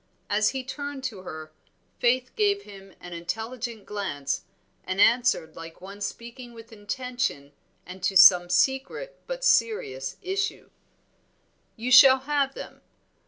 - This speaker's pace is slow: Yes, slow, 130 wpm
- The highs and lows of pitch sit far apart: Yes, wide, 6.1 semitones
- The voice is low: No, high, 230 Hz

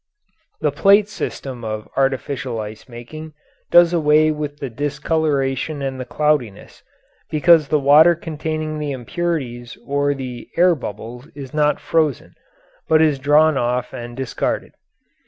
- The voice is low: No, medium, 145 Hz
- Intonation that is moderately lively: Yes, average, 3.8 semitones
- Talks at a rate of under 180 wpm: Yes, slow, 135 wpm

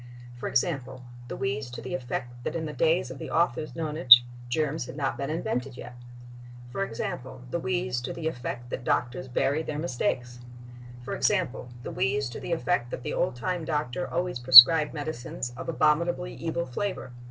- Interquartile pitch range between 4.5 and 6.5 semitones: Yes, average, 4.9 semitones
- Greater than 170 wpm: Yes, average, 180 wpm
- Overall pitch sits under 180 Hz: Yes, medium, 140 Hz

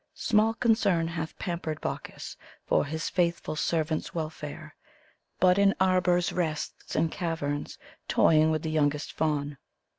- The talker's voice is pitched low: No, medium, 165 Hz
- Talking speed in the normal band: No, slow, 125 wpm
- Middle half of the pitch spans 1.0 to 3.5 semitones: Yes, average, 2.8 semitones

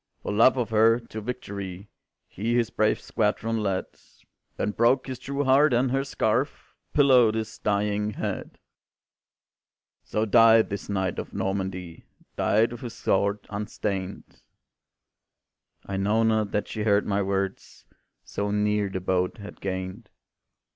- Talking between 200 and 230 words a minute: No, average, 140 wpm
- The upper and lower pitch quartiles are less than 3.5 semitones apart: Yes, average, 2.7 semitones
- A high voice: No, low, 105 Hz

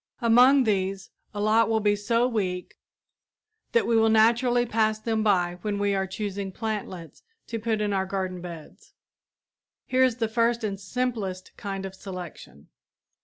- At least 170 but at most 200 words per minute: No, average, 160 wpm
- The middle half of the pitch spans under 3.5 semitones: Yes, average, 3.0 semitones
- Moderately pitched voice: No, high, 210 Hz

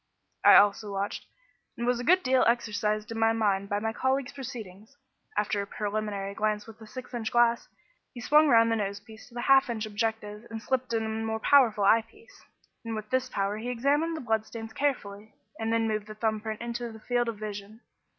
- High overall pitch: Yes, high, 225 Hz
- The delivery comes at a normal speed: No, fast, 215 wpm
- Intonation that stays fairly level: Yes, narrow, 2.3 semitones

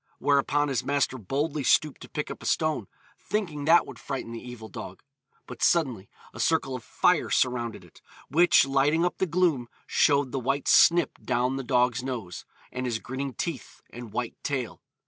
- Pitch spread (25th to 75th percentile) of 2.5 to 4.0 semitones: Yes, average, 3.4 semitones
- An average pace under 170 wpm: No, average, 180 wpm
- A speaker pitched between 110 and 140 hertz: Yes, low, 135 Hz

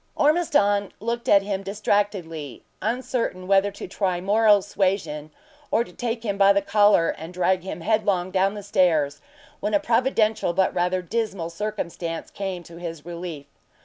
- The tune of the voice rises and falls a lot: No, average, 3.1 semitones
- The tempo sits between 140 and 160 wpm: Yes, average, 155 wpm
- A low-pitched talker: No, high, 195 Hz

